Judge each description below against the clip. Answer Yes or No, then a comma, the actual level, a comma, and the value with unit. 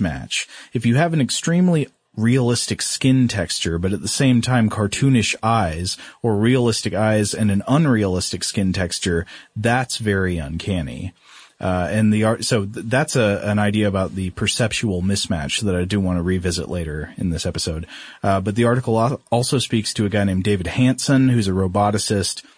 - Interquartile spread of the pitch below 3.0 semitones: No, average, 4.2 semitones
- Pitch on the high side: No, low, 105 Hz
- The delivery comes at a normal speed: Yes, average, 175 wpm